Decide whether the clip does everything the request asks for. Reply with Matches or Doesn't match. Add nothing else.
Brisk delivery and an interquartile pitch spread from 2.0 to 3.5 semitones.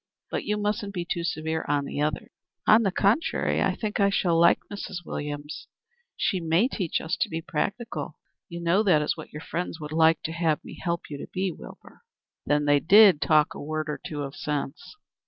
Doesn't match